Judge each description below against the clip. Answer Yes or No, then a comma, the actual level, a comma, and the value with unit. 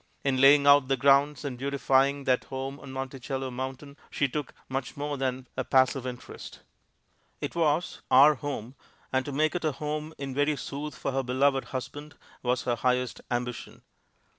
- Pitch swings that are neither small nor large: No, narrow, 1.8 semitones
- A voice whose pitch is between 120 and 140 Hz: Yes, low, 135 Hz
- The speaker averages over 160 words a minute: Yes, average, 170 wpm